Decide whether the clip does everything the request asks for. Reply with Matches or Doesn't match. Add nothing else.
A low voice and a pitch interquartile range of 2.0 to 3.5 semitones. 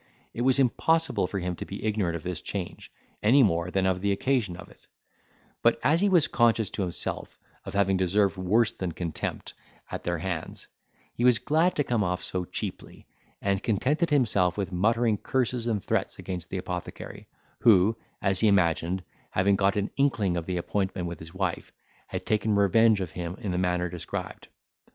Doesn't match